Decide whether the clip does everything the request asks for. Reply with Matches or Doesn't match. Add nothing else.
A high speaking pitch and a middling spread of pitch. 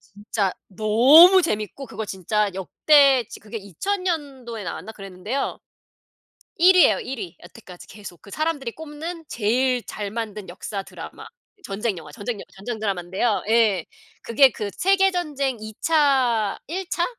Doesn't match